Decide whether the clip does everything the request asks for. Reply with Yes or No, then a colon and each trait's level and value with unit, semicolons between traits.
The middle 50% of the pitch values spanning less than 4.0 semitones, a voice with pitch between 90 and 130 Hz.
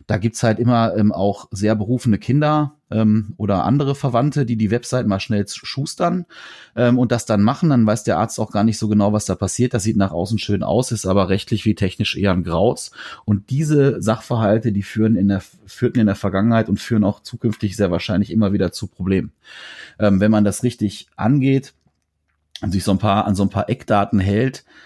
Yes: average, 3.1 semitones; low, 110 Hz